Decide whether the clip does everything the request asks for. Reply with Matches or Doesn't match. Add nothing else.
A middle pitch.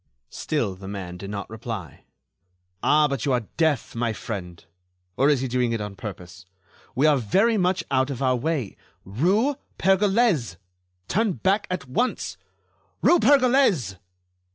Doesn't match